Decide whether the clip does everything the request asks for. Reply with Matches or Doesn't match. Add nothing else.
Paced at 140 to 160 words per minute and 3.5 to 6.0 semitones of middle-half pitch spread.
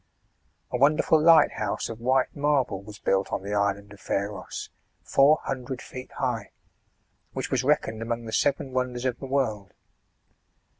Matches